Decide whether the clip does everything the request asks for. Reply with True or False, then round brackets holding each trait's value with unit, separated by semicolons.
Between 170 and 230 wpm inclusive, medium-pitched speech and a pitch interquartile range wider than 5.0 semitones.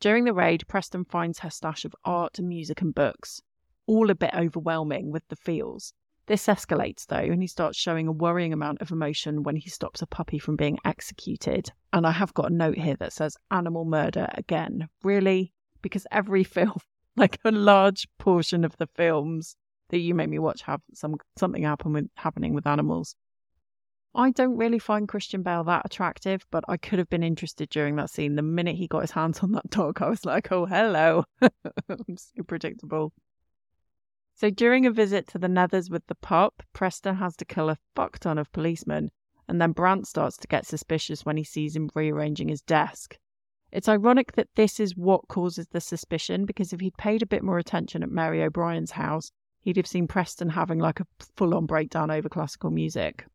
False (200 wpm; 170 Hz; 3.8 semitones)